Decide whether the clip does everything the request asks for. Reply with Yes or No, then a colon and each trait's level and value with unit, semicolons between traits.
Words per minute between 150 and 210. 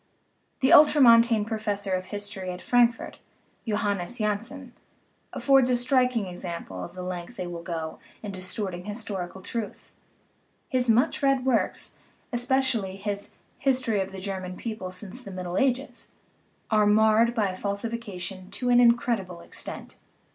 No: average, 140 wpm